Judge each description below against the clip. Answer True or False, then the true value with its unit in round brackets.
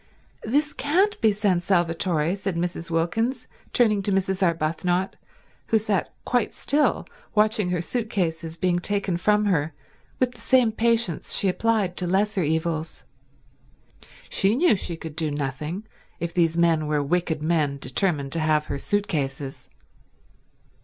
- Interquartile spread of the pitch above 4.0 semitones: True (4.6 semitones)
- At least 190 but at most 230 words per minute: False (145 wpm)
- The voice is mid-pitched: True (180 Hz)